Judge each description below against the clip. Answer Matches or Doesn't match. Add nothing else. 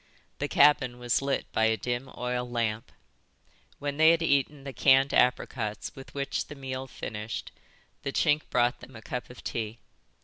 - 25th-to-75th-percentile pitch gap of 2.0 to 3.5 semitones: Matches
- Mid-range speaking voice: Doesn't match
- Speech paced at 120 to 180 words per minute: Matches